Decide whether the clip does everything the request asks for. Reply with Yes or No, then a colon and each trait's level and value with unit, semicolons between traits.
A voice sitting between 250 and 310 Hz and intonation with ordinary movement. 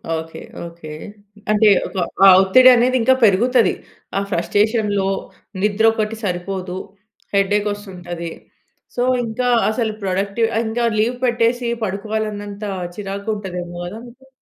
No: high, 205 Hz; average, 3.0 semitones